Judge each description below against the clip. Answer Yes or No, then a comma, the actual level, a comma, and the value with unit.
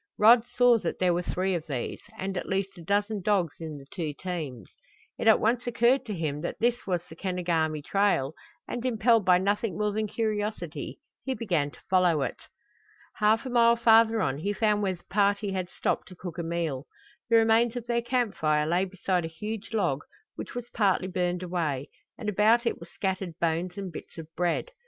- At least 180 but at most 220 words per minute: Yes, fast, 205 wpm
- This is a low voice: No, high, 190 Hz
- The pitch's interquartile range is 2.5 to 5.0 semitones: Yes, average, 4.7 semitones